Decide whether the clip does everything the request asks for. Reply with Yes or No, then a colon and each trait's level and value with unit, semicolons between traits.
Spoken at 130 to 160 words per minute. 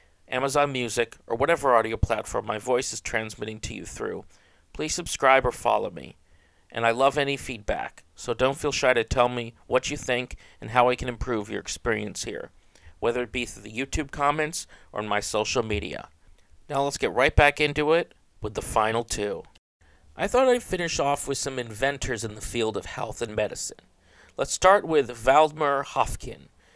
No: average, 190 wpm